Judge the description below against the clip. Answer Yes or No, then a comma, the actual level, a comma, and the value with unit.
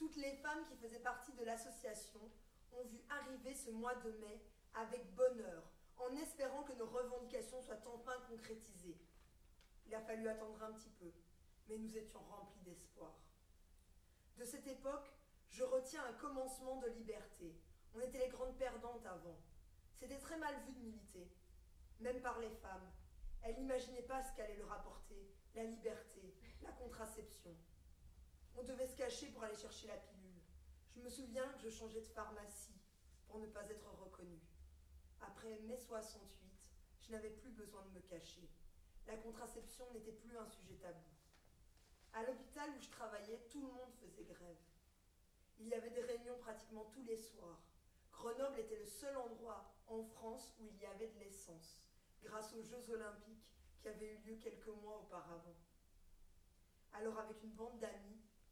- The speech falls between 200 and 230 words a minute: No, average, 165 wpm